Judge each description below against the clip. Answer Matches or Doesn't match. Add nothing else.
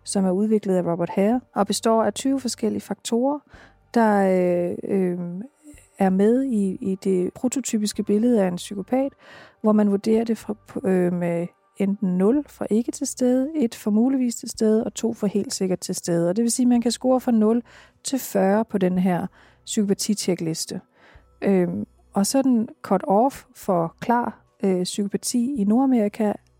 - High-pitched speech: Matches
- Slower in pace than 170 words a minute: Doesn't match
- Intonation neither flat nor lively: Matches